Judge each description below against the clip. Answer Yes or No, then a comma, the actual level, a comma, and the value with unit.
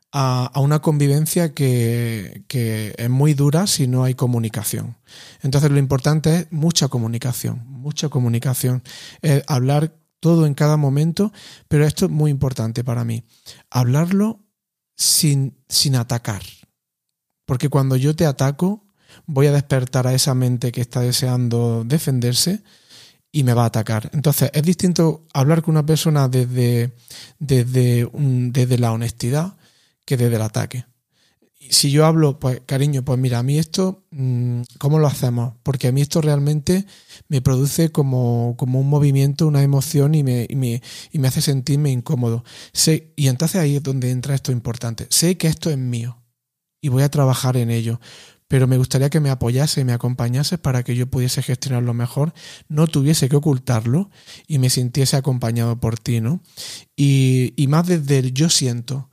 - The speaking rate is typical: Yes, average, 165 wpm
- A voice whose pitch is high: No, low, 135 Hz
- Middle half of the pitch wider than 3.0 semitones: Yes, average, 3.4 semitones